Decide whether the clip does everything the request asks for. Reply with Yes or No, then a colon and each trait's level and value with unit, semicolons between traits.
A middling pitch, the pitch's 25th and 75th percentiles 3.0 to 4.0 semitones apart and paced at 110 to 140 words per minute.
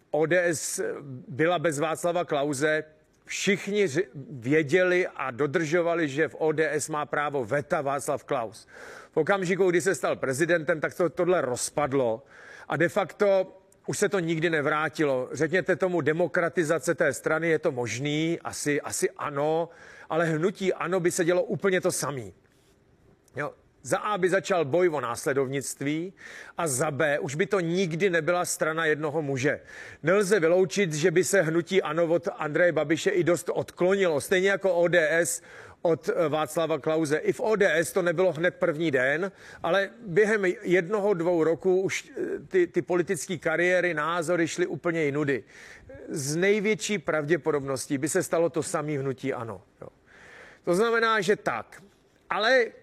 No: medium, 170 Hz; average, 3.3 semitones; average, 150 wpm